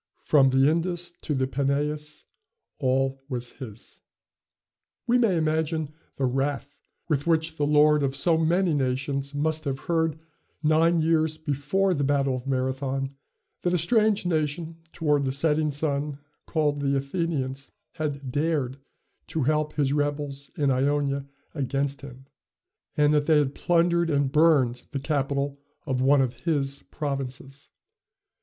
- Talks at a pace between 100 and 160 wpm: Yes, average, 140 wpm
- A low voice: No, medium, 145 Hz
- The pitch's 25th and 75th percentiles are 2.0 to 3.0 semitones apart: Yes, narrow, 2.6 semitones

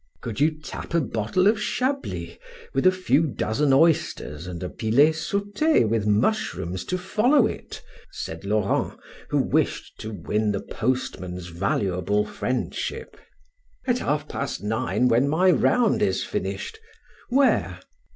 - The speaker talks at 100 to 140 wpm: Yes, slow, 135 wpm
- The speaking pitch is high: No, low, 130 Hz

